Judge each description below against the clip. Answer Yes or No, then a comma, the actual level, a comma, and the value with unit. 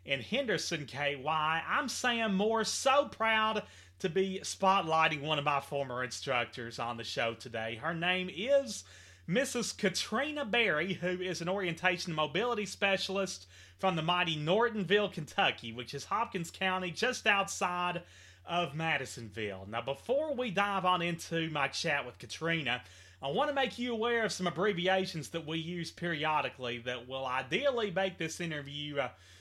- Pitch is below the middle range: No, medium, 170 Hz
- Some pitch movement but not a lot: No, wide, 6.3 semitones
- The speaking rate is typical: Yes, average, 155 wpm